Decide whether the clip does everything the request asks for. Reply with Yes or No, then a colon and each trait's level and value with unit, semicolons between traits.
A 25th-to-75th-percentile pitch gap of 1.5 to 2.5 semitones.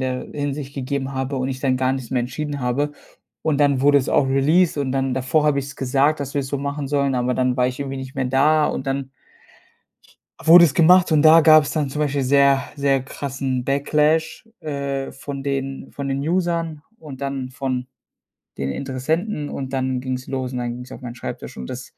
Yes: narrow, 2.0 semitones